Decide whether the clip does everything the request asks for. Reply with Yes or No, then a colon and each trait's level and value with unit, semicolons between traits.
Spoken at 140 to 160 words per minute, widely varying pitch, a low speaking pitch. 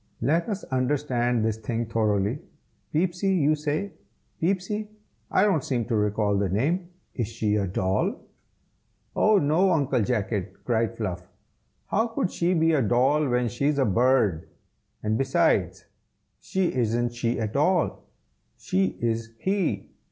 Yes: average, 145 wpm; wide, 6.7 semitones; low, 125 Hz